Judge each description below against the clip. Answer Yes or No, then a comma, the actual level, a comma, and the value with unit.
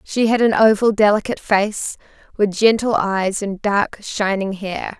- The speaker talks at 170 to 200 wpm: No, average, 155 wpm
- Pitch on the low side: No, high, 205 Hz